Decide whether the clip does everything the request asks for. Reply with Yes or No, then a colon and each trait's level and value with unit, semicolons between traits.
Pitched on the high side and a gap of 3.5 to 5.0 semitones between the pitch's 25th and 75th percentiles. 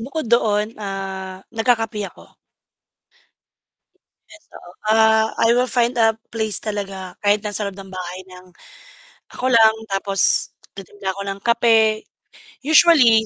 No: high, 215 Hz; average, 3.0 semitones